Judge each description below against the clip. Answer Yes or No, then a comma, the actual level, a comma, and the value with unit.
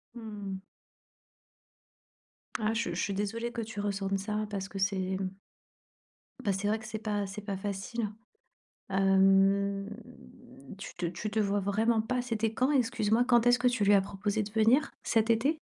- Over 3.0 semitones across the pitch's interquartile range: No, narrow, 2.4 semitones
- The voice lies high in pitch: Yes, high, 210 Hz